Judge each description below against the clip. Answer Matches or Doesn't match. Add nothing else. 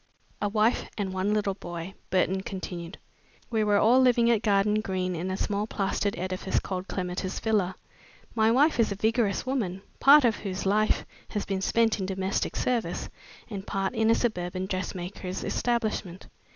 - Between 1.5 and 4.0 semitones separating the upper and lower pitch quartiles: Matches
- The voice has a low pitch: Doesn't match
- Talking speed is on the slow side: Doesn't match